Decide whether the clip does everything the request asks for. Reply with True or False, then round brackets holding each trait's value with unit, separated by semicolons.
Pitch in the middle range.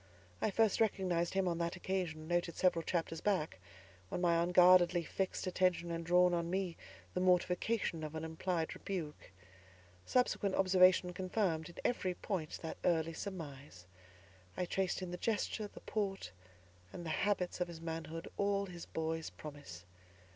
True (175 Hz)